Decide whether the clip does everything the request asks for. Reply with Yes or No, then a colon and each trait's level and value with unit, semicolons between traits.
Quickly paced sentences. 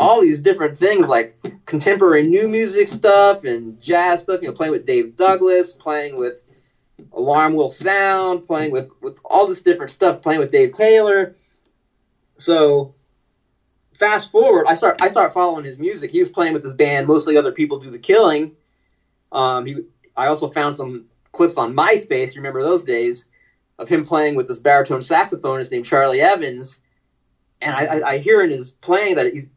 No: average, 180 wpm